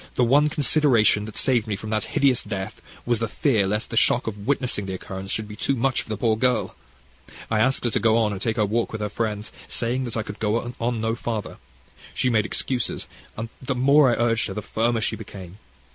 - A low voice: Yes, low, 115 Hz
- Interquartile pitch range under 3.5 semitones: Yes, average, 2.7 semitones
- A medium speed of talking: No, fast, 220 wpm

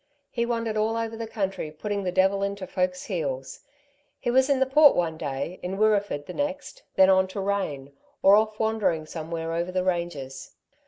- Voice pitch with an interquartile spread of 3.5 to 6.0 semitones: Yes, average, 4.6 semitones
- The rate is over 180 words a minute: Yes, average, 190 wpm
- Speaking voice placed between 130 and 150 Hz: No, high, 190 Hz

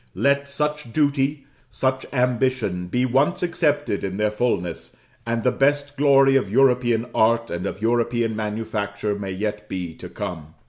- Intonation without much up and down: No, average, 4.7 semitones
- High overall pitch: No, low, 120 Hz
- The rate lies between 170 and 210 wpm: No, average, 150 wpm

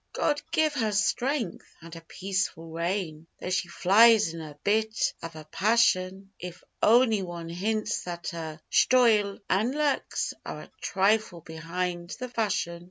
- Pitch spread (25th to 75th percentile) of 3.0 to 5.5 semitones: Yes, average, 4.6 semitones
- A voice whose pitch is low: No, high, 190 Hz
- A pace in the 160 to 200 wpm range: No, average, 150 wpm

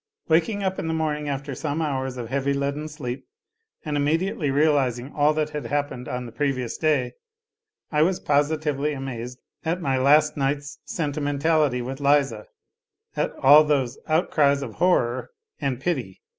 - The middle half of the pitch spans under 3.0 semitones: Yes, narrow, 2.4 semitones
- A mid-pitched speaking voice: Yes, medium, 145 Hz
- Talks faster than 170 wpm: No, average, 155 wpm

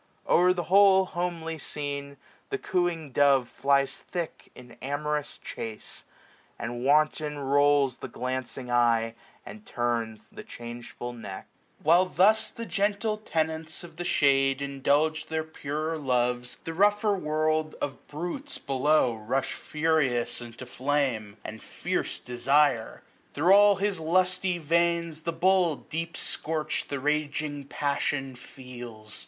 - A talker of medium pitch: Yes, medium, 150 Hz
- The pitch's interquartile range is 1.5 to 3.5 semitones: No, average, 4.7 semitones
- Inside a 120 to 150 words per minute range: Yes, slow, 135 wpm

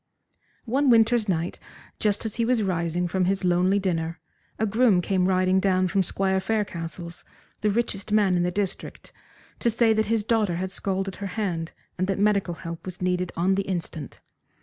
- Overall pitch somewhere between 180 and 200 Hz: Yes, high, 190 Hz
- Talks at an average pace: Yes, average, 180 wpm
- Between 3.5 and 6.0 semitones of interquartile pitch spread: No, average, 2.9 semitones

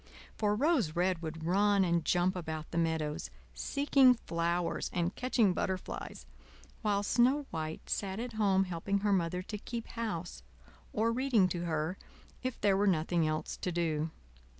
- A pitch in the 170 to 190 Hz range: Yes, medium, 185 Hz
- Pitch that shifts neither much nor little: Yes, average, 4.2 semitones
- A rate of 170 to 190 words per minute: No, average, 155 wpm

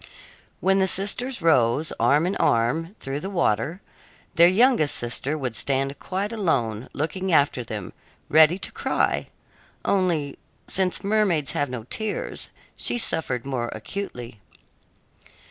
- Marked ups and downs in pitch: Yes, wide, 7.2 semitones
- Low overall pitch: No, medium, 155 Hz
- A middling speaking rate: No, slow, 130 wpm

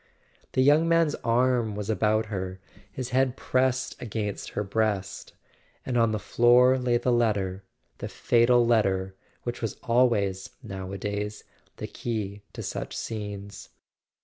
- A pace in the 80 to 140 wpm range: Yes, slow, 135 wpm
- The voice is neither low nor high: No, low, 110 Hz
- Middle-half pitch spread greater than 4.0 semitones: No, average, 3.4 semitones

